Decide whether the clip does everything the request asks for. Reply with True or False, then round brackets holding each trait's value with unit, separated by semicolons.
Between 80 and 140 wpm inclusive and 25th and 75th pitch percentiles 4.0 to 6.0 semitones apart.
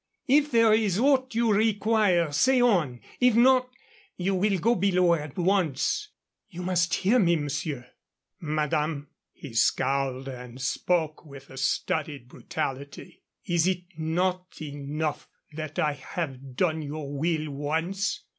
True (135 wpm; 5.4 semitones)